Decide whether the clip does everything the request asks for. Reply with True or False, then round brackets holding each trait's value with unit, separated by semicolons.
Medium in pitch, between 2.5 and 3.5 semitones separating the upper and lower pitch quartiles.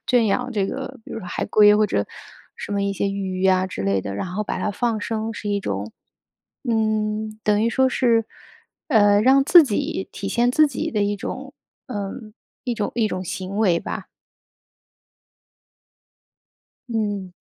False (210 Hz; 3.0 semitones)